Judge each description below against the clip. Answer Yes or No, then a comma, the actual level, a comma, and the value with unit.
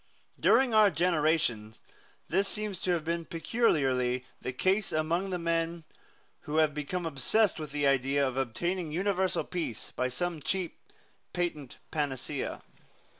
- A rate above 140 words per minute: No, slow, 135 wpm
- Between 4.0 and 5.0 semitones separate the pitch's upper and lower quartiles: Yes, average, 4.6 semitones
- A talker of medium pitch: Yes, medium, 165 Hz